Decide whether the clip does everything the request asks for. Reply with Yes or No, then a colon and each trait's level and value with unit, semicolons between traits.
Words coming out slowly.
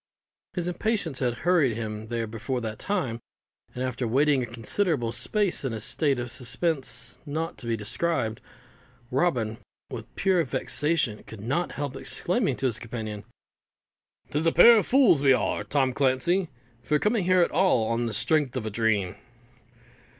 No: average, 165 wpm